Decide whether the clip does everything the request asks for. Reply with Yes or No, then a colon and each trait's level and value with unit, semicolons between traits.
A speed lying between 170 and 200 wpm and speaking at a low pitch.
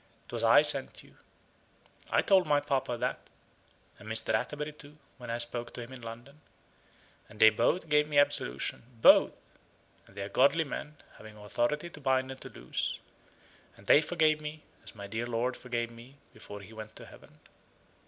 Yes: average, 180 wpm; low, 125 Hz